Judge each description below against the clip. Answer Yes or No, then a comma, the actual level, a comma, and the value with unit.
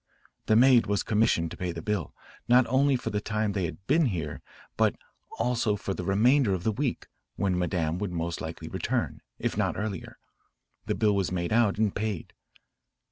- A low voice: Yes, low, 105 Hz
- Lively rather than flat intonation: No, average, 4.2 semitones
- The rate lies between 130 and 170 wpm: No, average, 190 wpm